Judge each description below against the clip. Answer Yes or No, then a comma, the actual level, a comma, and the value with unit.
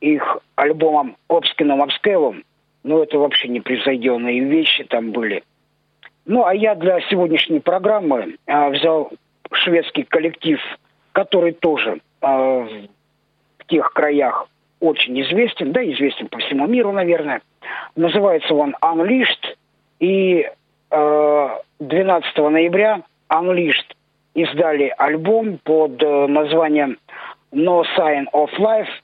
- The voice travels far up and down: No, average, 4.2 semitones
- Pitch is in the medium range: Yes, medium, 160 Hz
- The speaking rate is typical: No, slow, 105 wpm